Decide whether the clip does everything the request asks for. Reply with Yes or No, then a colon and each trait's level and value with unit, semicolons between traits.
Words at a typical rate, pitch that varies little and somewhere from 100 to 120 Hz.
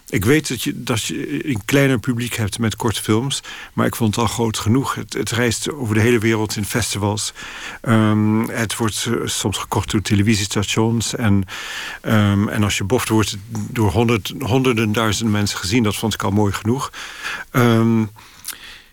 Yes: average, 180 wpm; narrow, 2.2 semitones; low, 110 Hz